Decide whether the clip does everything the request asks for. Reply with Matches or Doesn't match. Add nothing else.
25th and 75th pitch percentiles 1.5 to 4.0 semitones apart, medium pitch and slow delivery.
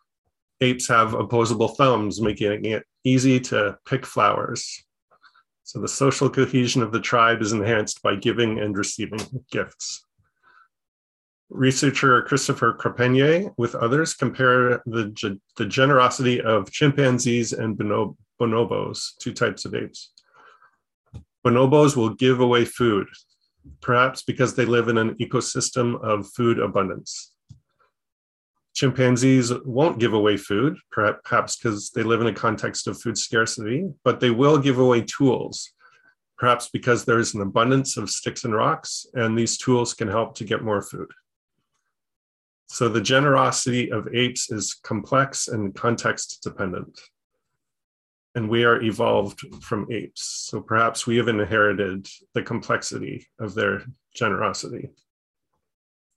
Doesn't match